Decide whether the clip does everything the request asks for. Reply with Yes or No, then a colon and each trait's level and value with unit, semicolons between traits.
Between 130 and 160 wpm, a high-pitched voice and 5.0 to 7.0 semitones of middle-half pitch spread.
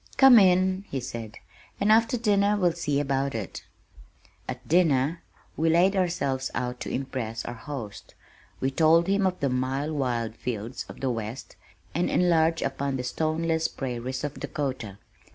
No: average, 155 wpm; medium, 140 Hz; wide, 5.4 semitones